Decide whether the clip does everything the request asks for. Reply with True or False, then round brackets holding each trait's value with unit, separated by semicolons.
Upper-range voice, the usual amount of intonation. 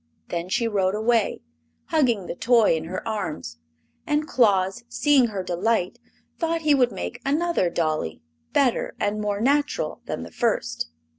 False (215 Hz; 6.3 semitones)